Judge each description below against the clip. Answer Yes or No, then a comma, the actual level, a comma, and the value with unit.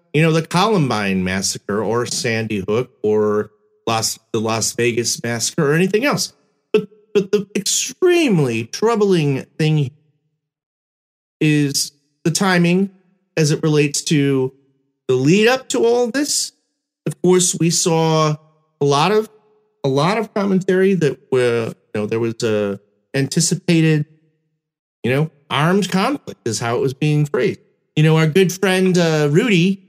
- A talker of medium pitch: Yes, medium, 155 Hz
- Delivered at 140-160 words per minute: Yes, average, 145 wpm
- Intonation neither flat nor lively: No, wide, 5.9 semitones